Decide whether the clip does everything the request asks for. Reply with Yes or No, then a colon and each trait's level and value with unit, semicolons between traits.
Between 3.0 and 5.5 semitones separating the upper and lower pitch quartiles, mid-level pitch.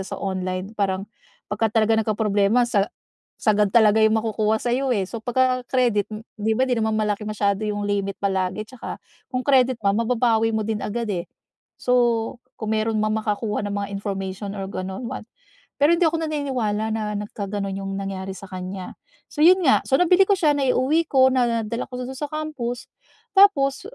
No: average, 3.9 semitones; high, 220 Hz